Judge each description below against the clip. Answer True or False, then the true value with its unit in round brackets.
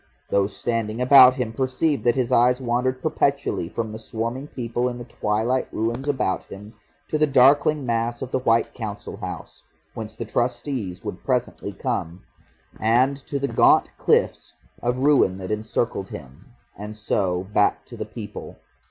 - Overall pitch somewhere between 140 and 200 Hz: False (120 Hz)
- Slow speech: False (160 wpm)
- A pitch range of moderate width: True (3.2 semitones)